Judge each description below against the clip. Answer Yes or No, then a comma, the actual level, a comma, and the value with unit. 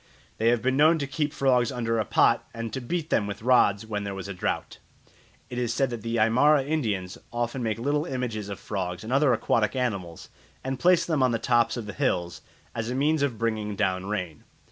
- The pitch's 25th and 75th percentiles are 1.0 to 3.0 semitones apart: No, average, 4.1 semitones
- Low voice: Yes, low, 115 Hz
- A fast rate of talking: Yes, fast, 220 wpm